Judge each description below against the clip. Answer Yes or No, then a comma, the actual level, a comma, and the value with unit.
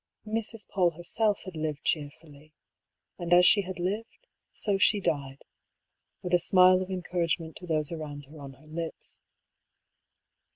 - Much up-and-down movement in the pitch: No, average, 3.4 semitones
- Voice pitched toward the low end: No, medium, 175 Hz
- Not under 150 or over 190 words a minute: Yes, average, 160 wpm